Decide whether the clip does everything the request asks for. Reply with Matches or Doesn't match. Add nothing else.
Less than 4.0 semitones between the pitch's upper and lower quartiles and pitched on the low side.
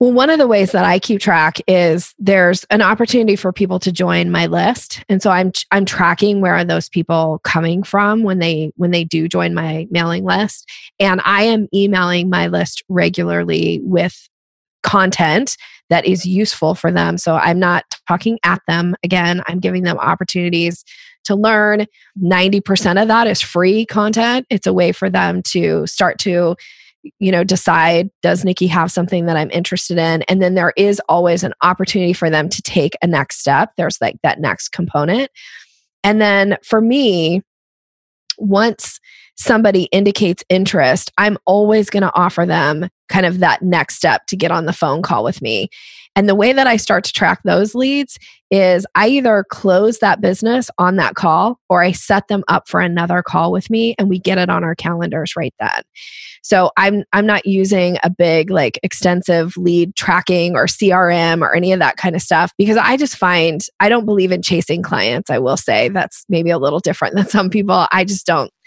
Doesn't match